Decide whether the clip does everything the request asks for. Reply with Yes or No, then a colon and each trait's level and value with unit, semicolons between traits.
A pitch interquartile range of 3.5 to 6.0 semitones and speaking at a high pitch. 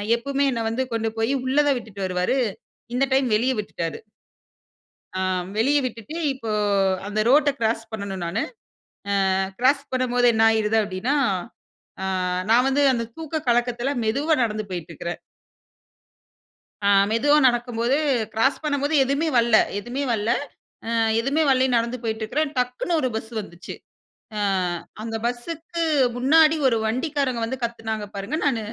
Yes: average, 3.8 semitones; high, 240 Hz